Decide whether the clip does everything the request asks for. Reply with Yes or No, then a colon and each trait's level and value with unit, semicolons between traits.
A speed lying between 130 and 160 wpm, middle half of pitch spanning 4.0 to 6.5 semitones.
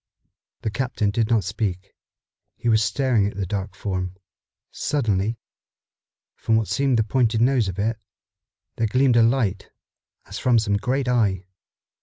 No: average, 150 wpm; average, 3.2 semitones